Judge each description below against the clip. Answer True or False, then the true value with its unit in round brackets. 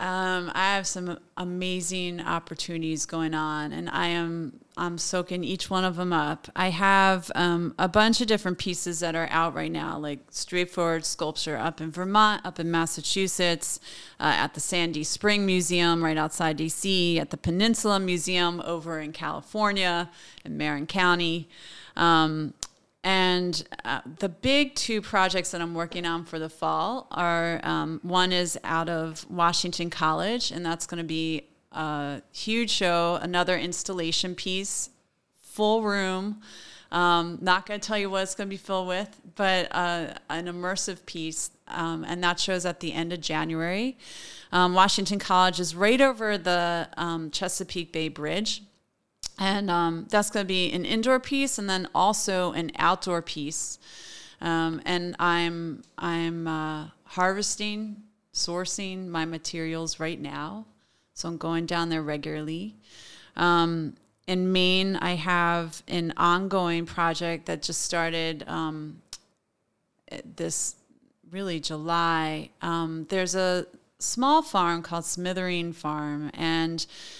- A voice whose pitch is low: False (175 Hz)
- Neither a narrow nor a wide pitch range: False (2.3 semitones)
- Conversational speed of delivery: True (145 wpm)